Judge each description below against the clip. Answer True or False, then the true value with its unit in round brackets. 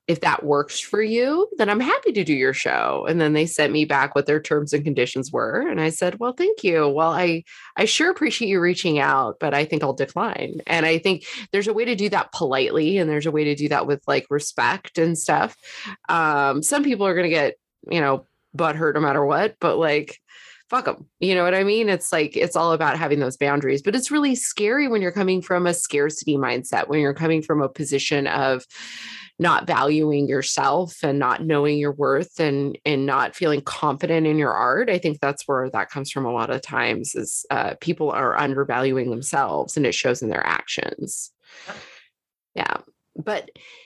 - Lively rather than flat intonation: False (4.1 semitones)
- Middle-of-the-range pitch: True (155 Hz)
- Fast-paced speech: True (210 wpm)